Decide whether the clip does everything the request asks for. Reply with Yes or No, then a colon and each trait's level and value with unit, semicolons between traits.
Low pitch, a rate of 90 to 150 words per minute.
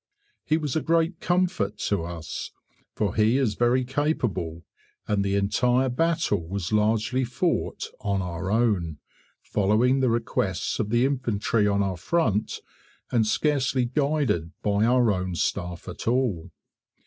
Yes: low, 110 Hz; average, 140 wpm